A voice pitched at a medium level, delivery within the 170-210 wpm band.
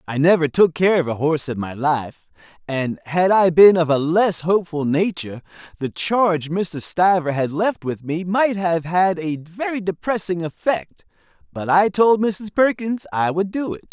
Yes: medium, 175 Hz; average, 185 wpm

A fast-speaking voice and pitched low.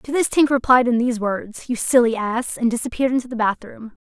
No: fast, 225 wpm; high, 240 Hz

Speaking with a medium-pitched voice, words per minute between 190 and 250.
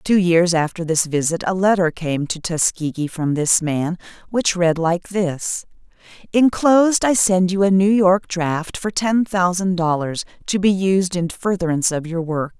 No: medium, 180 Hz; average, 175 wpm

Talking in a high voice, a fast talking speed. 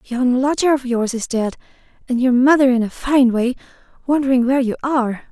No: very high, 255 Hz; average, 190 wpm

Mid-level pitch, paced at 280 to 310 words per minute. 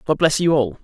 Yes: medium, 150 Hz; fast, 290 wpm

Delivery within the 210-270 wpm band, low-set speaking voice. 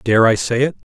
Yes: fast, 265 wpm; low, 120 Hz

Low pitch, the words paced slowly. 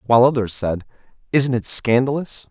Yes: low, 120 Hz; slow, 120 wpm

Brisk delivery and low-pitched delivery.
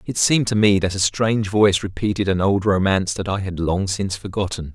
Yes: fast, 225 wpm; low, 100 Hz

